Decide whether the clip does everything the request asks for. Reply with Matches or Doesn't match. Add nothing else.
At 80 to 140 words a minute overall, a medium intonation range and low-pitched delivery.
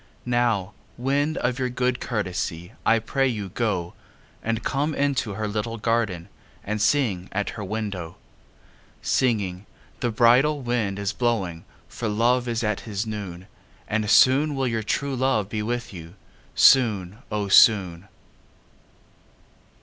Matches